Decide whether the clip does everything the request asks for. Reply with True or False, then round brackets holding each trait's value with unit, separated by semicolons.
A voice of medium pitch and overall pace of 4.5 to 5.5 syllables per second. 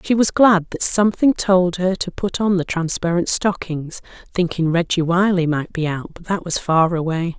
True (175 Hz; 4.7 syllables/s)